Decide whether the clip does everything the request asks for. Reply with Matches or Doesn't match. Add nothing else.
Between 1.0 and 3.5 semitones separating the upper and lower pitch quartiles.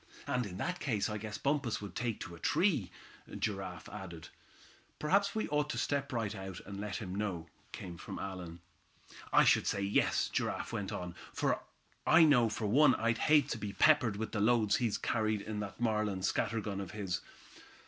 Doesn't match